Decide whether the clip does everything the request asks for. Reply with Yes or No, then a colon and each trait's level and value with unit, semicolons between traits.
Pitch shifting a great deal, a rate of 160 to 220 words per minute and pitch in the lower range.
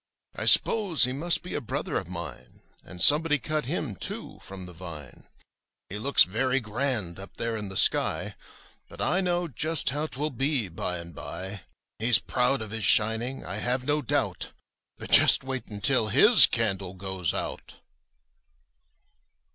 Yes: wide, 6.9 semitones; average, 165 wpm; low, 115 Hz